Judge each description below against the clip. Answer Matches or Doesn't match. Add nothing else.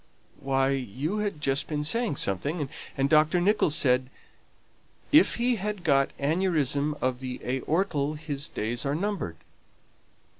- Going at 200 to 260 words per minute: Doesn't match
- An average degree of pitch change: Matches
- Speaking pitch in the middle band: Matches